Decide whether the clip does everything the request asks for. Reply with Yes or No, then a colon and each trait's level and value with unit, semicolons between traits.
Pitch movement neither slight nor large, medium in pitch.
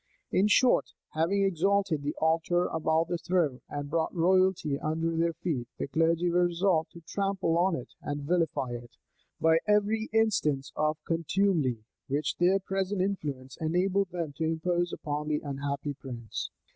Yes: average, 3.9 semitones; medium, 165 Hz